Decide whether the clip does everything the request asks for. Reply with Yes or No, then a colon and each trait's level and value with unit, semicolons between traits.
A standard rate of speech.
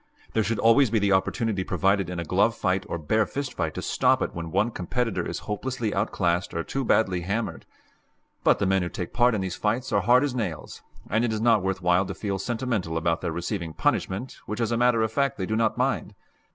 No: fast, 230 wpm